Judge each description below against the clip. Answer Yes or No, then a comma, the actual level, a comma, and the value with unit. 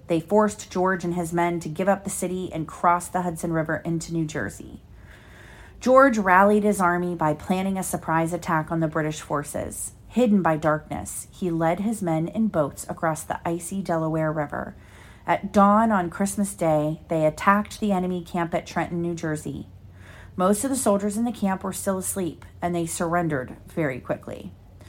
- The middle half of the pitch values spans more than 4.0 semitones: No, average, 3.4 semitones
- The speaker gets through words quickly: No, average, 180 wpm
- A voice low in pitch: No, medium, 175 Hz